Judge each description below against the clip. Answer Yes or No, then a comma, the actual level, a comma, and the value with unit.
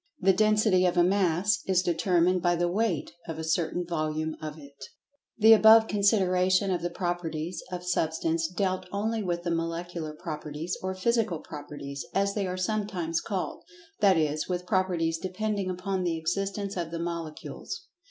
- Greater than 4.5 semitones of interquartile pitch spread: No, average, 3.1 semitones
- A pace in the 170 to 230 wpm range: No, average, 160 wpm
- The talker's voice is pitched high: No, medium, 180 Hz